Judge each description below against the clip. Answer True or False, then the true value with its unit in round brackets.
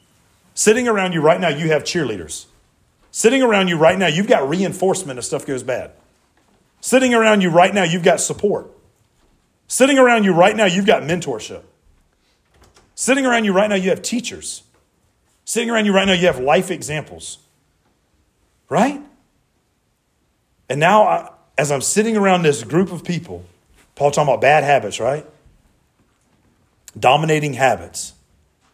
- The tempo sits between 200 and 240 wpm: False (150 wpm)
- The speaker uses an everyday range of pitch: False (7.6 semitones)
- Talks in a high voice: False (180 Hz)